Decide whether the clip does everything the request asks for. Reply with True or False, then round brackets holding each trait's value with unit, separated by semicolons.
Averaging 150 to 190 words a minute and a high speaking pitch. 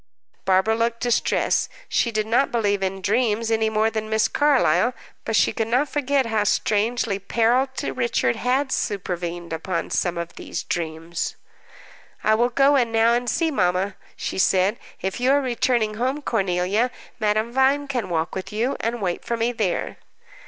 True (170 wpm; 225 Hz)